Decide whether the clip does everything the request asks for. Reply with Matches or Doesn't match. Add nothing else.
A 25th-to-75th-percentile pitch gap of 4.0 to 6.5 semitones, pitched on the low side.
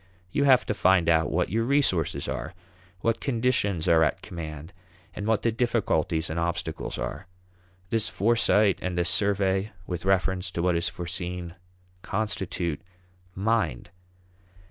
Matches